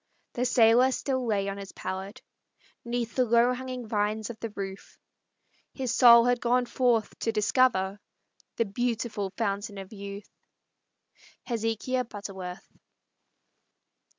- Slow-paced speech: Yes, slow, 125 wpm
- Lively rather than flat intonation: No, average, 3.5 semitones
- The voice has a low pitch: No, high, 225 Hz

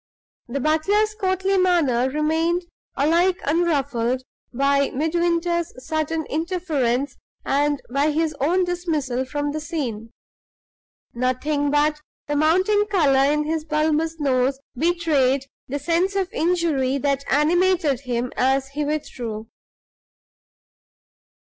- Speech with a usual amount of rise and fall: Yes, average, 3.9 semitones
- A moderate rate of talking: No, slow, 110 wpm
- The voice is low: No, very high, 300 Hz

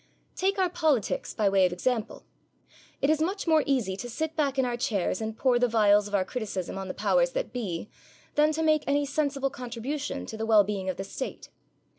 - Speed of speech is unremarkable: No, fast, 215 wpm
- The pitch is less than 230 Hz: No, very high, 250 Hz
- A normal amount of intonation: No, wide, 6.4 semitones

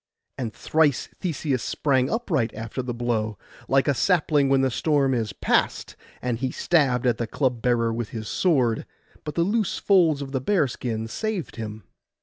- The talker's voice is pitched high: No, low, 130 Hz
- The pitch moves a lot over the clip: No, average, 4.7 semitones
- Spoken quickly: No, average, 170 wpm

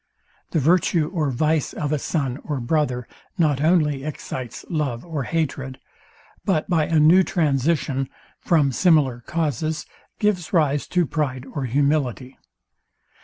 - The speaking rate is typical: No, slow, 130 wpm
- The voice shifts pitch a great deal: No, average, 3.2 semitones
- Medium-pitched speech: Yes, medium, 150 Hz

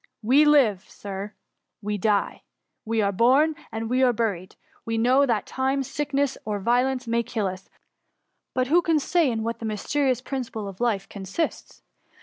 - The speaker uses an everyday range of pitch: Yes, average, 4.1 semitones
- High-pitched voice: Yes, high, 235 Hz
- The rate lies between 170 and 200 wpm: Yes, average, 175 wpm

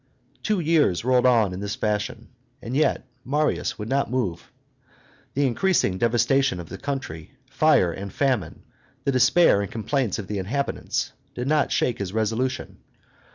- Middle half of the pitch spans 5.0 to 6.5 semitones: Yes, wide, 5.4 semitones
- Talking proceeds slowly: No, average, 155 wpm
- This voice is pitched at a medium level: No, low, 120 Hz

